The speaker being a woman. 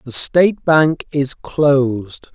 No: male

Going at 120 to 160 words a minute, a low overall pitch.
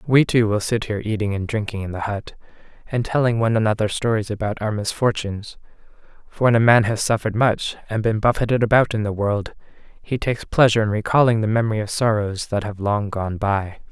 No: fast, 205 wpm; low, 110 Hz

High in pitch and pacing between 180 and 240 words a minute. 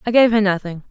No: high, 205 Hz; fast, 265 wpm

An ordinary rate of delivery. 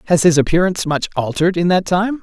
No: fast, 215 wpm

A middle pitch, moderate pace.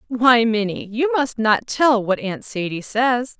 No: high, 230 Hz; average, 175 wpm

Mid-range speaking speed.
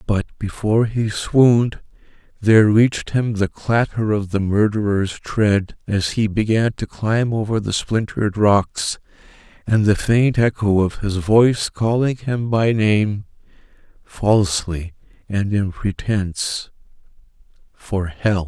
No: slow, 120 wpm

